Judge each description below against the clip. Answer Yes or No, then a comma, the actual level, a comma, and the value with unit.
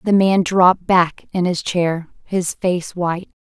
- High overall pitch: No, medium, 180 Hz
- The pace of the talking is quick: No, average, 170 wpm